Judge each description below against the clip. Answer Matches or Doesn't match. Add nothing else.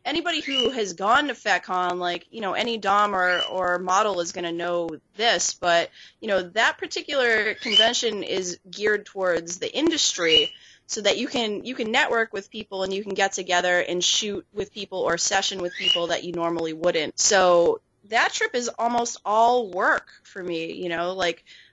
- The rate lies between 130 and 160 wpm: Doesn't match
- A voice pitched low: Doesn't match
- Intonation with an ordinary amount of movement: Matches